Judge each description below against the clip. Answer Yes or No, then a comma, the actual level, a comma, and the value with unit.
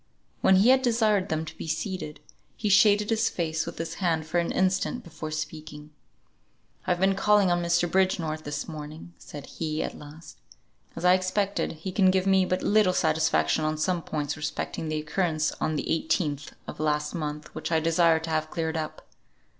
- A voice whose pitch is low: No, medium, 165 Hz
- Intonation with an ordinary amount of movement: Yes, average, 3.3 semitones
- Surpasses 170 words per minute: Yes, average, 190 wpm